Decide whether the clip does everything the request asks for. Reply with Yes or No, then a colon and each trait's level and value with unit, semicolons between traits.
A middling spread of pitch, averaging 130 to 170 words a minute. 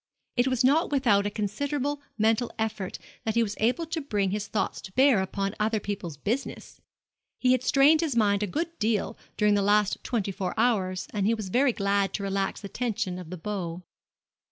No: average, 4.2 semitones; average, 200 wpm